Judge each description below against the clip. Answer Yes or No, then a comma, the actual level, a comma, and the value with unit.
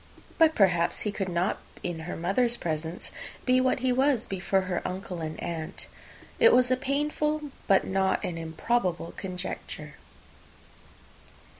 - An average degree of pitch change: No, wide, 6.7 semitones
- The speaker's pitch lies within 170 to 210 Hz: Yes, high, 190 Hz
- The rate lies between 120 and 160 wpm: Yes, average, 140 wpm